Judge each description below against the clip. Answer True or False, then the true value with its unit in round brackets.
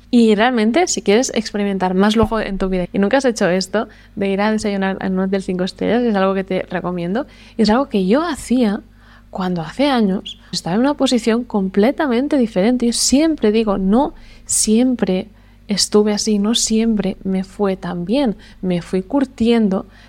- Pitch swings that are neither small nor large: True (3.7 semitones)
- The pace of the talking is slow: False (175 wpm)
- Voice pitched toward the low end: False (210 Hz)